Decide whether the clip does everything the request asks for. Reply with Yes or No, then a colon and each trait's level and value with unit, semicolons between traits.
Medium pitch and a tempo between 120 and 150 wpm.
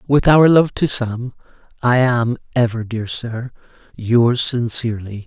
No: low, 120 Hz; slow, 135 wpm